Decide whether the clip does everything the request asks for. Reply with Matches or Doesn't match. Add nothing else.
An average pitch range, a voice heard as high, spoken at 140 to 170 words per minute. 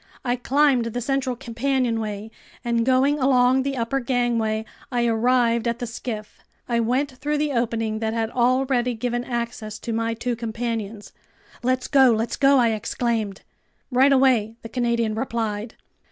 Doesn't match